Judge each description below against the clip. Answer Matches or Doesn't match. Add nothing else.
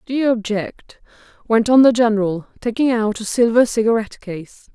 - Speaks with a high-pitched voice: Matches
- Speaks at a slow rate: Doesn't match